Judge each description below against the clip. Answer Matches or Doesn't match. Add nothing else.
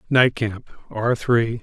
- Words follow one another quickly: Doesn't match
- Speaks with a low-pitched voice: Matches